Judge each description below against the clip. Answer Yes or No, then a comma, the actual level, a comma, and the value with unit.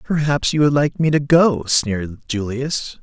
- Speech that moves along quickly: No, average, 180 wpm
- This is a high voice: No, low, 135 Hz